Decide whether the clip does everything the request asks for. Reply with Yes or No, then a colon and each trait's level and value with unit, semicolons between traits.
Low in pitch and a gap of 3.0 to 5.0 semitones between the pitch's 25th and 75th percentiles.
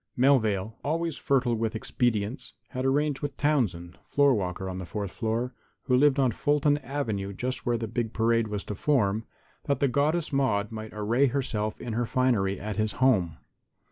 Yes: low, 120 Hz; average, 4.5 semitones